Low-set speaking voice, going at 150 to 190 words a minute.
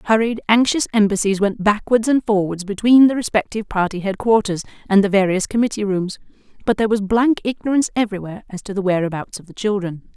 No: high, 205 Hz; average, 175 wpm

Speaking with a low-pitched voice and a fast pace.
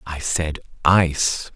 No: very low, 80 Hz; slow, 115 wpm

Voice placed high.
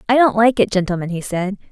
Yes: high, 205 Hz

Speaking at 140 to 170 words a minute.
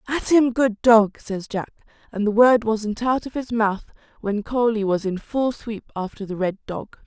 No: fast, 205 wpm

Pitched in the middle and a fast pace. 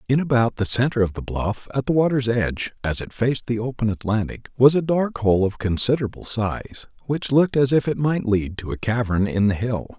No: low, 120 Hz; fast, 220 wpm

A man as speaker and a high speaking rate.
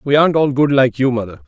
Yes: male; fast, 285 wpm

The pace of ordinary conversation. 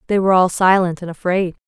No: fast, 215 wpm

